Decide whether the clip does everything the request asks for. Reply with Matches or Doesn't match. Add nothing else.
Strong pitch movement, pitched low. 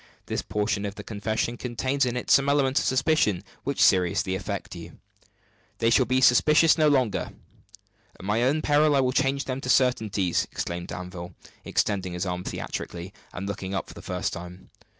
Matches